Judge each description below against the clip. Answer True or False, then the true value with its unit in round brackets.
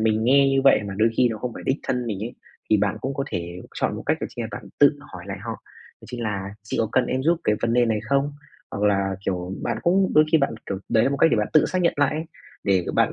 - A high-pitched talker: False (115 Hz)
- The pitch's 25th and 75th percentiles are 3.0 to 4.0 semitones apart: False (5.2 semitones)